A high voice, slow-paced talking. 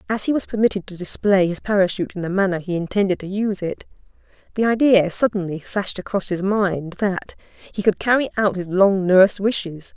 No: high, 195 Hz; average, 195 wpm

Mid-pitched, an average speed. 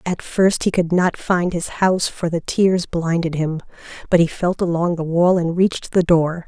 No: medium, 175 Hz; fast, 215 wpm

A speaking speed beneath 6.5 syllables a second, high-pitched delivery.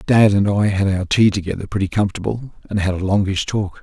No: 5.9 syllables/s; low, 100 Hz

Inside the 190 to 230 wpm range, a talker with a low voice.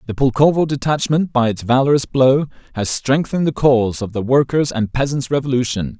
No: average, 170 wpm; low, 130 Hz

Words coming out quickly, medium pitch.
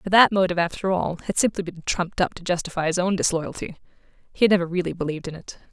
Yes: fast, 230 wpm; medium, 175 Hz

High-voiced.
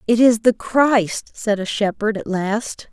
Yes: high, 220 Hz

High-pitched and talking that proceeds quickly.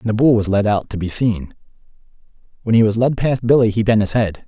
No: low, 110 Hz; fast, 255 wpm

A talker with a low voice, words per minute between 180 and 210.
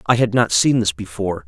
No: low, 115 Hz; fast, 245 wpm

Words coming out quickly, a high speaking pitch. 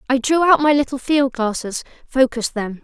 No: average, 190 wpm; very high, 260 Hz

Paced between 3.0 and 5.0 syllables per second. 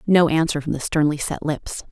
No: 5.2 syllables/s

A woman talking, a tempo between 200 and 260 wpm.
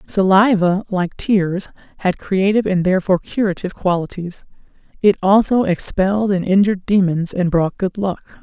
No: female; slow, 135 wpm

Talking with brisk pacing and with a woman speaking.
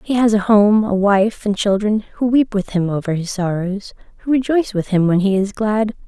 Yes: fast, 225 wpm; female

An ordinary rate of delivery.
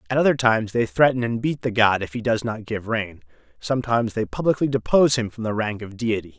No: fast, 235 wpm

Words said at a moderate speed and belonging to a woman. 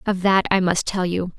No: fast, 260 wpm; female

